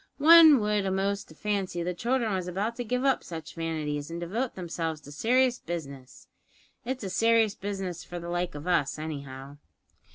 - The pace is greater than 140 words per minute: Yes, average, 170 wpm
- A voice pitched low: No, medium, 180 Hz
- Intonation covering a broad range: Yes, wide, 5.8 semitones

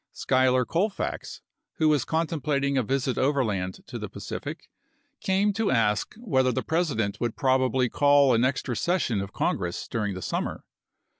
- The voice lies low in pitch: Yes, low, 130 Hz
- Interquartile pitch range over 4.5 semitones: Yes, average, 4.9 semitones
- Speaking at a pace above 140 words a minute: Yes, average, 150 wpm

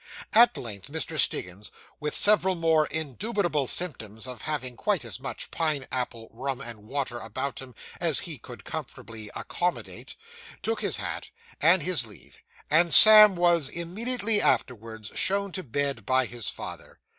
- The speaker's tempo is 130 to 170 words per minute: Yes, average, 150 wpm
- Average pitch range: No, wide, 6.9 semitones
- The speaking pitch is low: No, medium, 145 Hz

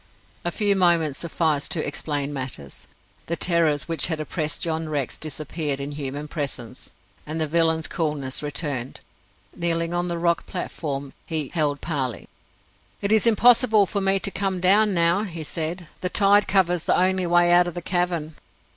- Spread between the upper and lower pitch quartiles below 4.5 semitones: Yes, average, 3.3 semitones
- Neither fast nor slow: Yes, average, 165 wpm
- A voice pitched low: No, medium, 165 Hz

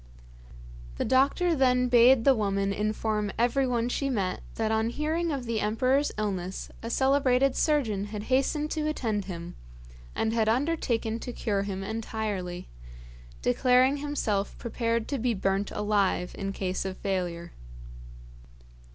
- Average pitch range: Yes, average, 4.6 semitones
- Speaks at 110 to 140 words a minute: Yes, slow, 135 wpm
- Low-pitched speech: No, high, 225 Hz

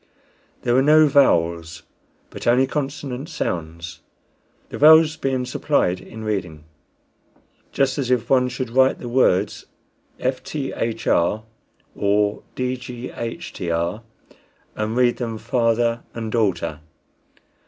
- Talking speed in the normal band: No, slow, 105 wpm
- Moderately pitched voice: No, low, 120 Hz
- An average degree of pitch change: Yes, average, 4.4 semitones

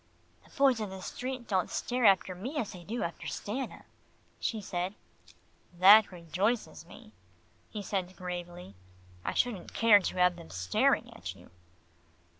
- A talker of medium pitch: No, high, 195 Hz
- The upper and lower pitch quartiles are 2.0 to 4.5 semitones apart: Yes, average, 4.2 semitones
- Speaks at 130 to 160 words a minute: Yes, average, 150 wpm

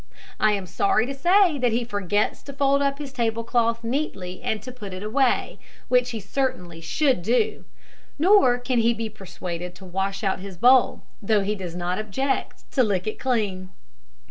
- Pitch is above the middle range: Yes, high, 225 Hz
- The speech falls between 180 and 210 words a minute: Yes, average, 185 wpm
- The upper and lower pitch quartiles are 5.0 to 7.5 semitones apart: Yes, average, 5.3 semitones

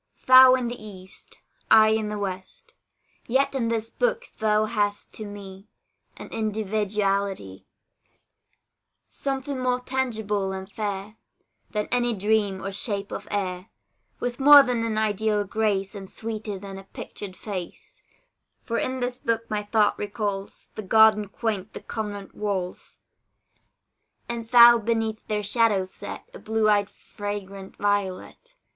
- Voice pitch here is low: No, high, 215 Hz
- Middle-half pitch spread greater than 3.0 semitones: No, narrow, 2.5 semitones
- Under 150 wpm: Yes, average, 140 wpm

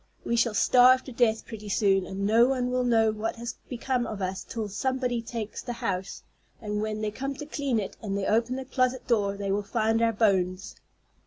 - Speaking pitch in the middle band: No, high, 225 Hz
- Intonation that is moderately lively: Yes, average, 3.2 semitones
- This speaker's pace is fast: Yes, fast, 215 wpm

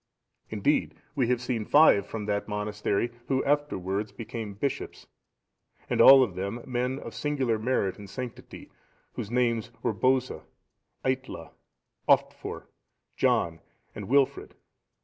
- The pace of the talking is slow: Yes, slow, 125 wpm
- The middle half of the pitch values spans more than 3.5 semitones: Yes, average, 3.9 semitones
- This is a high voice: No, low, 115 Hz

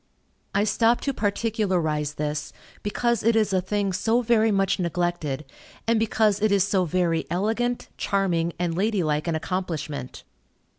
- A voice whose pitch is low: No, high, 195 Hz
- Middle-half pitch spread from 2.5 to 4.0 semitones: No, average, 4.6 semitones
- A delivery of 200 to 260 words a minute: No, average, 150 wpm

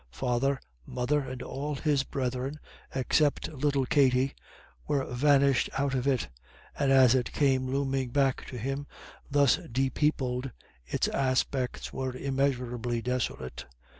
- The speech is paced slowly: Yes, slow, 125 wpm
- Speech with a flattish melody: Yes, narrow, 1.8 semitones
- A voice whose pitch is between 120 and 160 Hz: Yes, low, 135 Hz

